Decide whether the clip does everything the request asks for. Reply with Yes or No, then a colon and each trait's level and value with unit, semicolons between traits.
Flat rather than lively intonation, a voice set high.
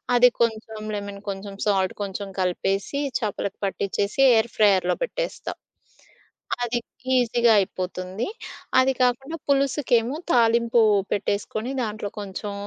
No: average, 3.4 semitones; high, 220 Hz